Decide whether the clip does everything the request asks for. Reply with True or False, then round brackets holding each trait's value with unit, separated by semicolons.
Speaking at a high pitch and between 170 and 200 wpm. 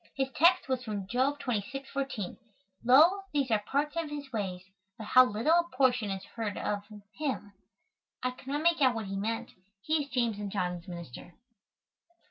True (250 Hz; 180 wpm)